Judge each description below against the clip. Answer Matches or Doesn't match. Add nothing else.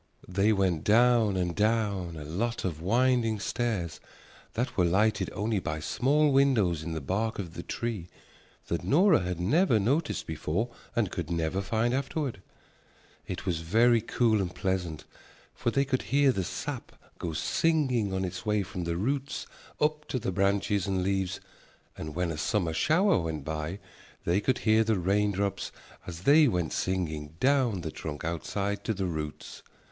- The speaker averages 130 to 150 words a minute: Doesn't match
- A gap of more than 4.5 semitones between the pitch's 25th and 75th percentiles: Matches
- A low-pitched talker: Matches